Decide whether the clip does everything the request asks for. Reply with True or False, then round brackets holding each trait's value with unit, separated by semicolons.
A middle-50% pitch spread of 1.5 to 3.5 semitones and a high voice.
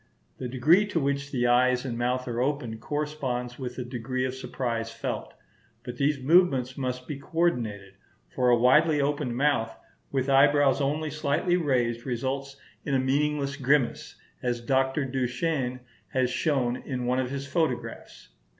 False (2.6 semitones; 130 Hz)